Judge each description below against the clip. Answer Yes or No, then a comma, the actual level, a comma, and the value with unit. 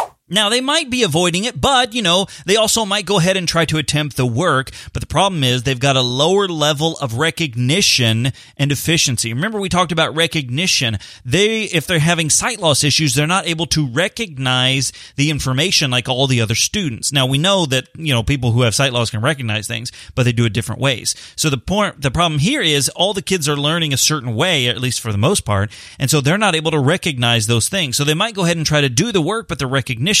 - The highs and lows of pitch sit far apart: Yes, wide, 5.7 semitones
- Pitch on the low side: No, medium, 150 Hz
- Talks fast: Yes, fast, 240 wpm